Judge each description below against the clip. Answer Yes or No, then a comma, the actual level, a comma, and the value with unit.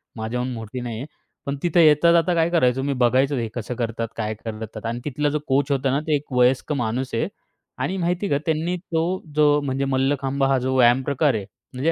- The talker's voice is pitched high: No, low, 135 Hz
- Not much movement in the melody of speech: No, average, 3.6 semitones